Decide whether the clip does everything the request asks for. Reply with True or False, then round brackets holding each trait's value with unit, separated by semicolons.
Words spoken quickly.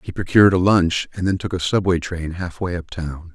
True (215 wpm)